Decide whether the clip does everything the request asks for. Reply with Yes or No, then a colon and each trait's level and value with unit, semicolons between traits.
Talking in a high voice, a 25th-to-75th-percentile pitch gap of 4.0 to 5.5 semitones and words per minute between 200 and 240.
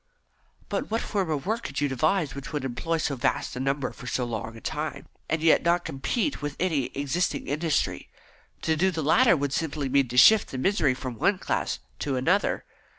No: medium, 150 Hz; average, 4.4 semitones; fast, 205 wpm